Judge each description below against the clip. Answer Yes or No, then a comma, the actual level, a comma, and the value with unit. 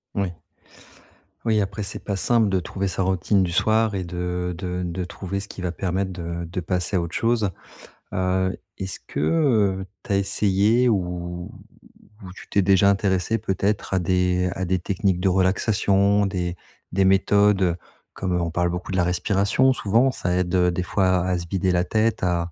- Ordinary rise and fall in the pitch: No, narrow, 2.1 semitones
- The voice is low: Yes, very low, 95 Hz